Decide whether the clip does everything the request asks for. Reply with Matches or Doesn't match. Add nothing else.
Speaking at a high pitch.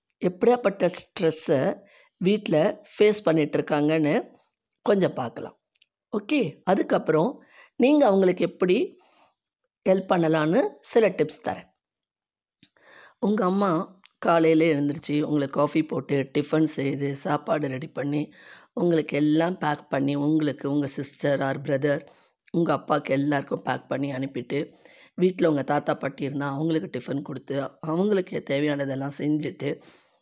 Doesn't match